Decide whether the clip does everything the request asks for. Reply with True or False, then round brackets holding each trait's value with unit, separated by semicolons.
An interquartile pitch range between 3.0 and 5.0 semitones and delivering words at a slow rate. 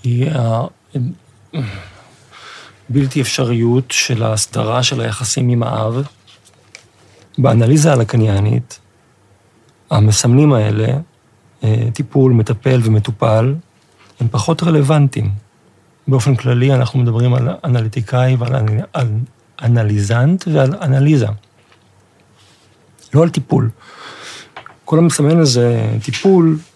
True (3.6 semitones; 80 wpm)